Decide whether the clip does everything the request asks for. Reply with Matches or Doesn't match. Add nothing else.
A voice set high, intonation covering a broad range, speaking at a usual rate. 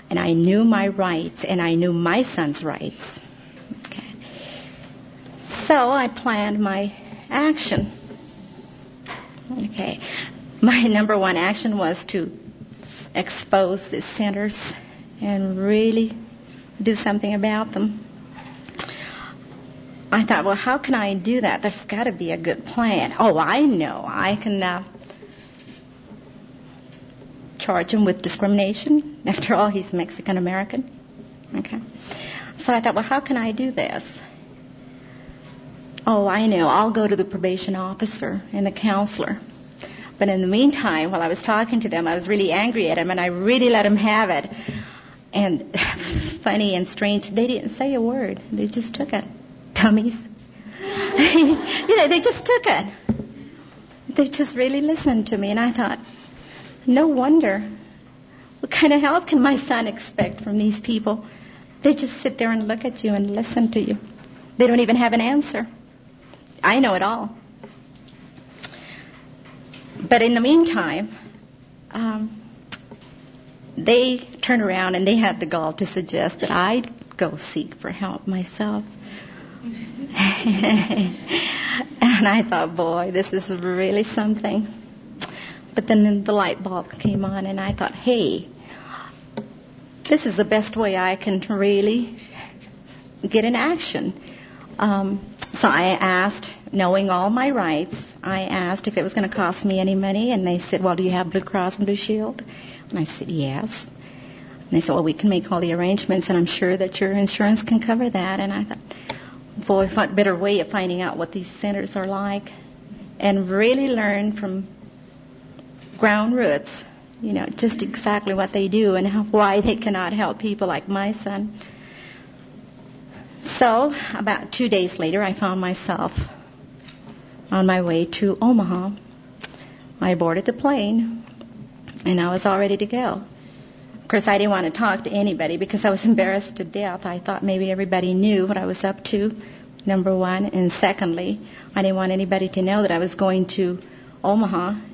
Doesn't match